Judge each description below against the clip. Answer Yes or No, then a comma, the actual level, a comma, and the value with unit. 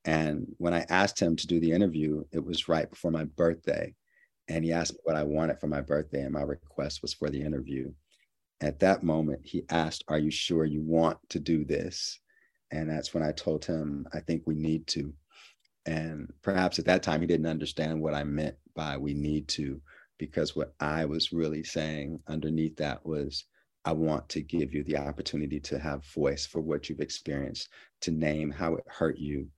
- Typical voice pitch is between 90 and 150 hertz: No, very low, 80 Hz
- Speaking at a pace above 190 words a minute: Yes, average, 200 wpm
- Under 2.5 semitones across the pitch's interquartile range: Yes, narrow, 1.7 semitones